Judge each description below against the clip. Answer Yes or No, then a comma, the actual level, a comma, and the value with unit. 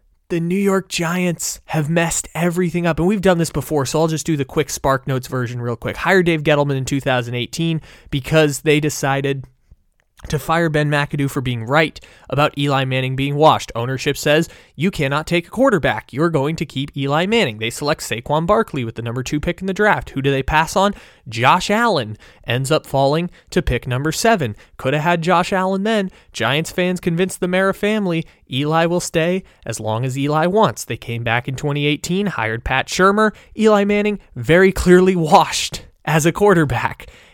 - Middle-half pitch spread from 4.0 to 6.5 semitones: Yes, average, 4.9 semitones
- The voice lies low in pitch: No, medium, 155 Hz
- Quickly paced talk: No, average, 190 wpm